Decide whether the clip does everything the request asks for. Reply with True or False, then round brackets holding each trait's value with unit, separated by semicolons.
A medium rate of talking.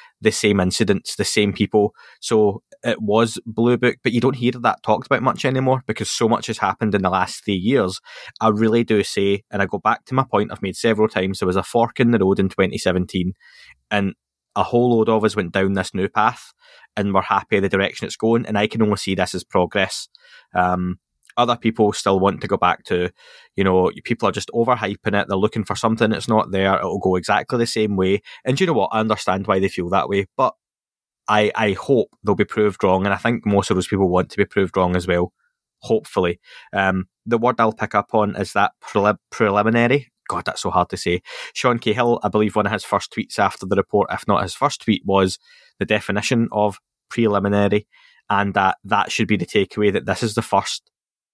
False (230 wpm)